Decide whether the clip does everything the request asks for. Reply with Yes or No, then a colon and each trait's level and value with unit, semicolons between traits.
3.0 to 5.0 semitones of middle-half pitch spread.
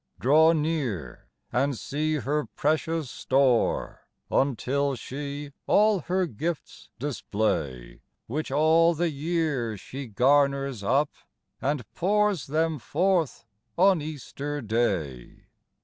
Yes: average, 4.3 semitones